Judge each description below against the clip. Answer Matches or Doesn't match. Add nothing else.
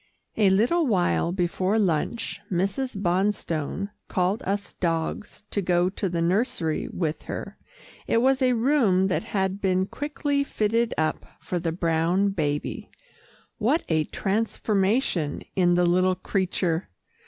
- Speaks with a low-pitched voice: Doesn't match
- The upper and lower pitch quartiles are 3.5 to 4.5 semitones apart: Matches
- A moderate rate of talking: Doesn't match